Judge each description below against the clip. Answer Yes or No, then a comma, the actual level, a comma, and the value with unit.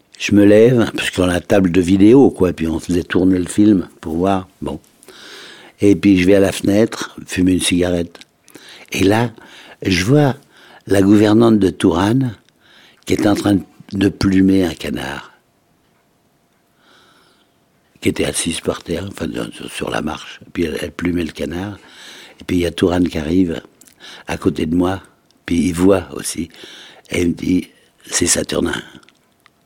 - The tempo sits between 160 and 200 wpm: Yes, average, 170 wpm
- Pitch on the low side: Yes, very low, 95 Hz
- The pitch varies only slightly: Yes, narrow, 2.2 semitones